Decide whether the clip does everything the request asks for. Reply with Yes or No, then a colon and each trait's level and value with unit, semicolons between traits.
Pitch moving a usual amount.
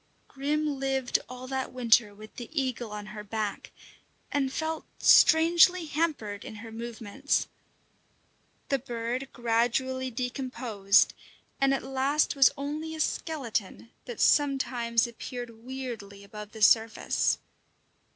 Yes: average, 3.5 semitones